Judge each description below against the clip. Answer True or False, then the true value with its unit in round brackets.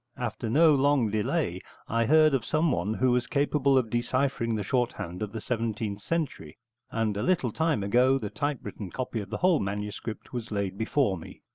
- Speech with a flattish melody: False (4.8 semitones)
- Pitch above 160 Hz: False (120 Hz)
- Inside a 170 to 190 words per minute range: True (180 wpm)